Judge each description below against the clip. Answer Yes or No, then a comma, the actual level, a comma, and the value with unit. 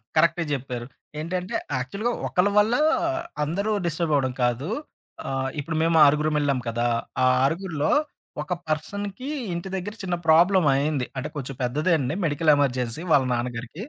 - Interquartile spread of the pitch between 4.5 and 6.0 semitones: Yes, average, 5.0 semitones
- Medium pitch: Yes, medium, 155 Hz